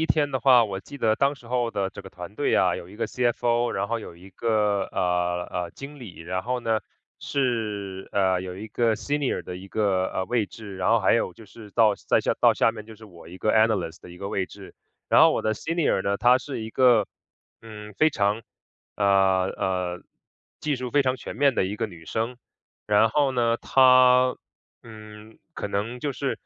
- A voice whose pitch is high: No, low, 110 Hz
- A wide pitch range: No, average, 4.1 semitones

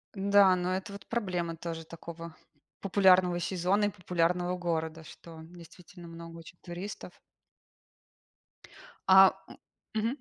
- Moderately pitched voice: Yes, medium, 180 Hz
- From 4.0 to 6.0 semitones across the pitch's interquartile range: No, narrow, 2.4 semitones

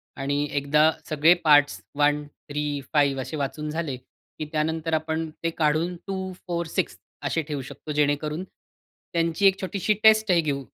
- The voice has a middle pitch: Yes, medium, 155 Hz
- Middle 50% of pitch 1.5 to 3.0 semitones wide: Yes, narrow, 2.4 semitones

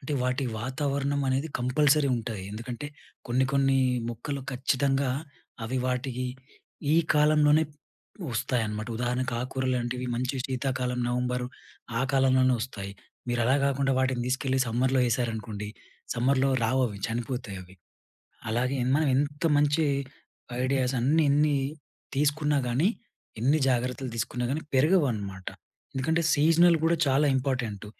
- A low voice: Yes, low, 130 Hz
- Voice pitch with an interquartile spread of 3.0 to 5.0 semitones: No, narrow, 2.5 semitones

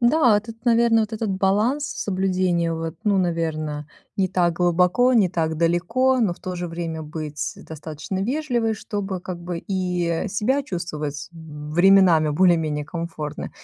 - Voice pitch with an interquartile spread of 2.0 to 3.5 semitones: No, average, 4.3 semitones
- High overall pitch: No, medium, 180 Hz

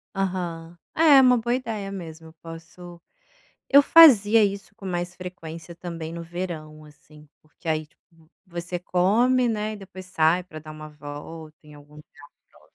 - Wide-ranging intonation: No, average, 3.8 semitones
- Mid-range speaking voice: Yes, medium, 175 Hz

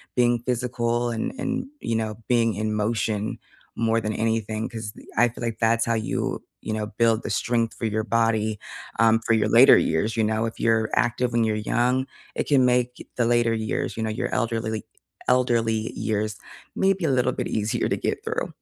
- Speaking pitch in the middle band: No, low, 115 Hz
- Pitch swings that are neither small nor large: No, narrow, 1.6 semitones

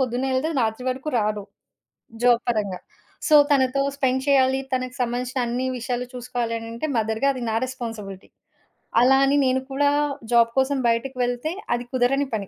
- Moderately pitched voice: No, very high, 250 Hz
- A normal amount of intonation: No, narrow, 2.3 semitones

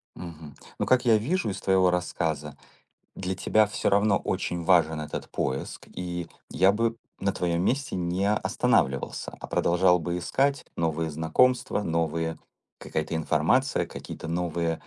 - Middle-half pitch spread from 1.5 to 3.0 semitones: No, average, 3.5 semitones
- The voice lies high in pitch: No, very low, 90 Hz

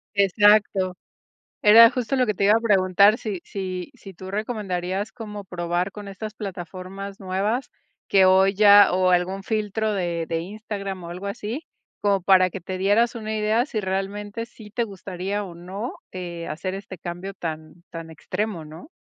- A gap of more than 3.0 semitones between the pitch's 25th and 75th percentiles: No, narrow, 2.5 semitones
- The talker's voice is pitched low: No, high, 195 Hz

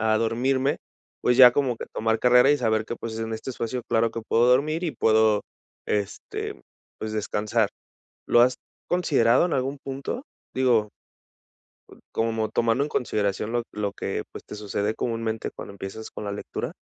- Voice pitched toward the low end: Yes, low, 115 Hz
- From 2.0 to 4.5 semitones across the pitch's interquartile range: Yes, narrow, 2.6 semitones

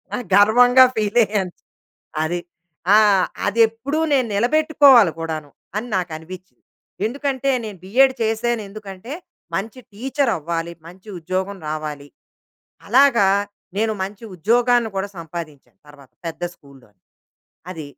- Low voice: No, high, 205 Hz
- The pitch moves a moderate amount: No, wide, 6.0 semitones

